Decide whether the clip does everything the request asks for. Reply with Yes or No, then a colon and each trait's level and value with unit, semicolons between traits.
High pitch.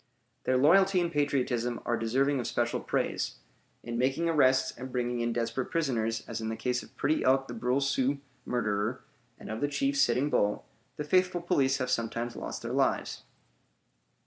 No: low, 130 Hz